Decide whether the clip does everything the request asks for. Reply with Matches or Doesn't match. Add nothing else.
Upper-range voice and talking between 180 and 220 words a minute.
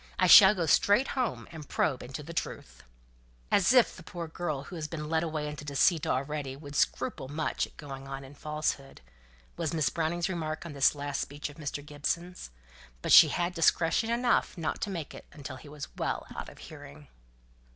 Doesn't match